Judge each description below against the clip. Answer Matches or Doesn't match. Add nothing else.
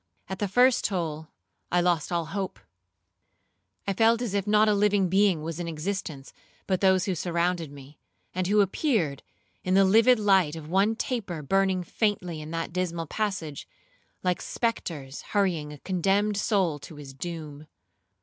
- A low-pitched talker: Doesn't match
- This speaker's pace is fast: Doesn't match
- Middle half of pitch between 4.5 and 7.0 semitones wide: Doesn't match